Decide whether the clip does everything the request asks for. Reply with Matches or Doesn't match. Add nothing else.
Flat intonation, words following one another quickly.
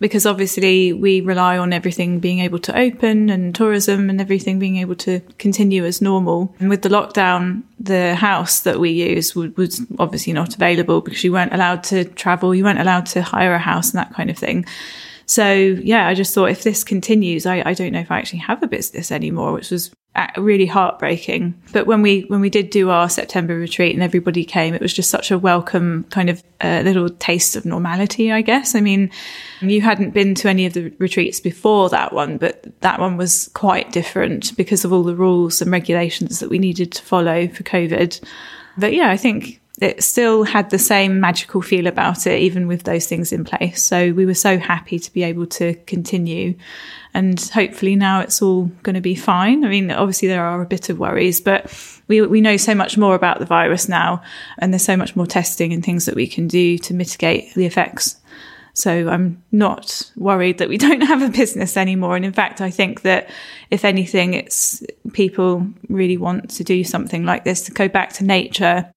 Matches